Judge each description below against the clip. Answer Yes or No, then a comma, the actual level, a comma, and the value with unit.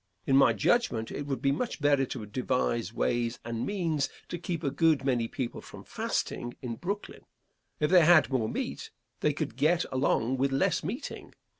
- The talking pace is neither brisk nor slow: Yes, average, 180 wpm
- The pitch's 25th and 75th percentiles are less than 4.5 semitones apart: No, average, 5.2 semitones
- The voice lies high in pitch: No, low, 135 Hz